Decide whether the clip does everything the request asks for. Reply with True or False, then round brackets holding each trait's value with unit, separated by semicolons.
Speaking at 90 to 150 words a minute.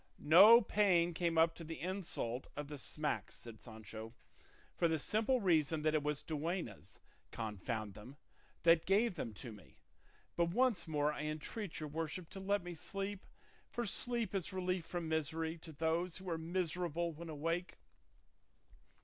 False (160 wpm)